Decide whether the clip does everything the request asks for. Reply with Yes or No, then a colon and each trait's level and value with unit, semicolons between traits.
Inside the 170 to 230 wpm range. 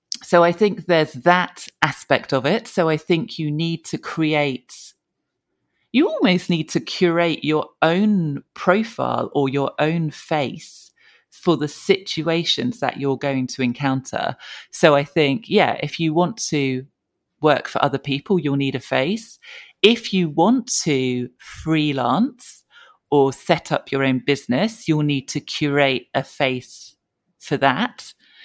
No: average, 150 wpm